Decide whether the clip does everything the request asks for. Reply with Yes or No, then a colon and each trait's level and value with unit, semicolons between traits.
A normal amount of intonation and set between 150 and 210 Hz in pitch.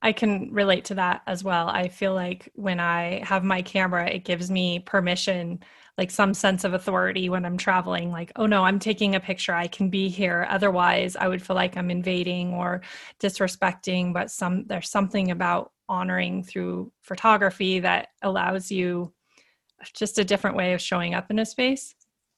No: narrow, 1.7 semitones; medium, 185 Hz